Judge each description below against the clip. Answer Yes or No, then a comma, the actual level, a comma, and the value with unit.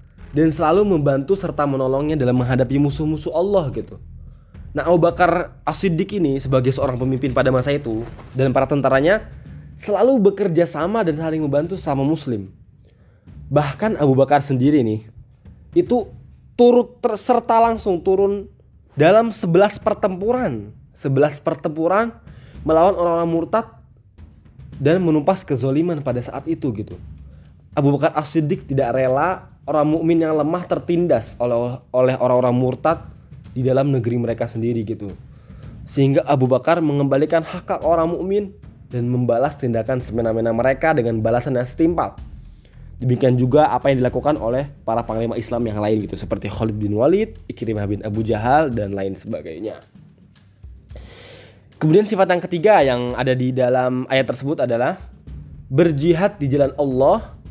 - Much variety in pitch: Yes, wide, 6.0 semitones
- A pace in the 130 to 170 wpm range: Yes, fast, 140 wpm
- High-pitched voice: No, low, 135 Hz